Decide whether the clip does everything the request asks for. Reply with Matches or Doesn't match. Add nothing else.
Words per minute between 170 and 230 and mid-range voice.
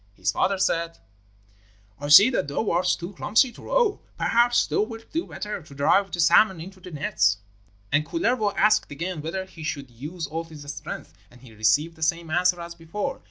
Matches